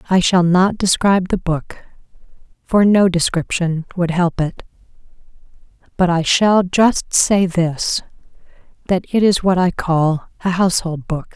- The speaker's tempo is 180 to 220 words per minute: No, average, 145 wpm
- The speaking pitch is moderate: Yes, medium, 180 Hz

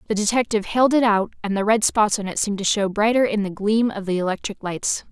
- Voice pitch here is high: Yes, high, 210 Hz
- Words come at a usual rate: No, fast, 260 wpm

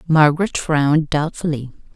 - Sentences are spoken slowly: Yes, slow, 90 wpm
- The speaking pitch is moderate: Yes, medium, 155 Hz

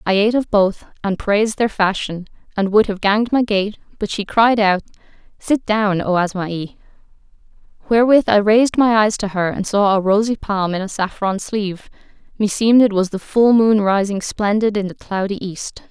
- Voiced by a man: No, female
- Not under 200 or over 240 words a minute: No, average, 190 wpm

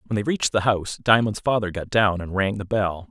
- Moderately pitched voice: No, low, 105 Hz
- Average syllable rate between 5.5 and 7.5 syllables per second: Yes, 5.9 syllables/s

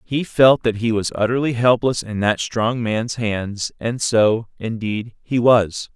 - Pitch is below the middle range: Yes, low, 115 Hz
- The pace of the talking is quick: No, average, 170 wpm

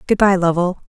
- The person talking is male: No, female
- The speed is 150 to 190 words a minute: No, average, 200 wpm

